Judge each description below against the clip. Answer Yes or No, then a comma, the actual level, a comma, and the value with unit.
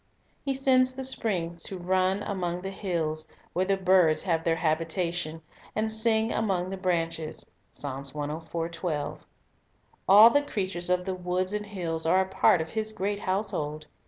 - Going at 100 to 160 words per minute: Yes, average, 155 wpm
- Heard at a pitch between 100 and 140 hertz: No, medium, 185 Hz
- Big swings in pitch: No, average, 3.7 semitones